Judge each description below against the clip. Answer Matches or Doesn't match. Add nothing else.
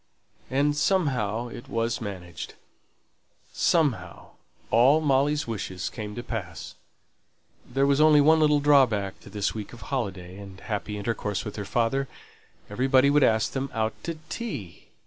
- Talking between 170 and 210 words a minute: Doesn't match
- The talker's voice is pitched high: Doesn't match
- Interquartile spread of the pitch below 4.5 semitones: Doesn't match